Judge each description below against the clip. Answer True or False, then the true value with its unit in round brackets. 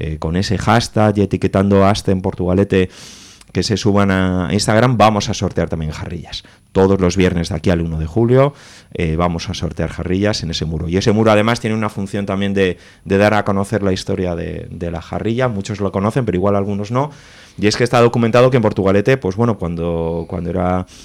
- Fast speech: True (215 wpm)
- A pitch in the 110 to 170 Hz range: False (95 Hz)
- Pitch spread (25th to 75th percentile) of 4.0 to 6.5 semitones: False (3.0 semitones)